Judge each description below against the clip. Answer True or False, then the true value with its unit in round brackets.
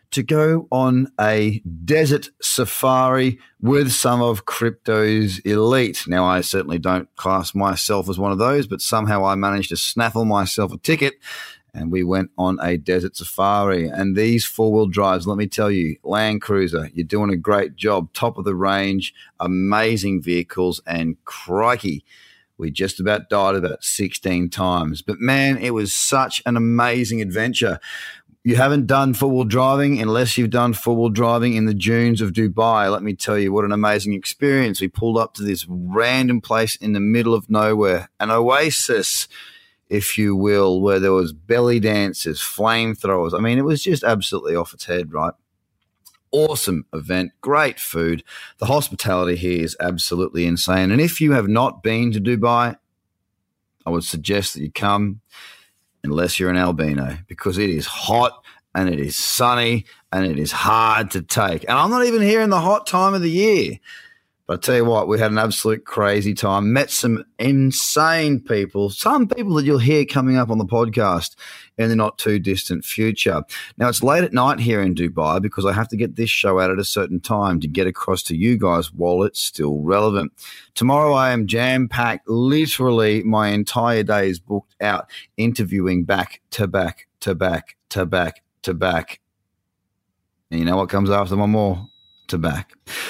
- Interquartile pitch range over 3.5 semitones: True (4.2 semitones)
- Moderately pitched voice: False (105 Hz)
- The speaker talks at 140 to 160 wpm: False (180 wpm)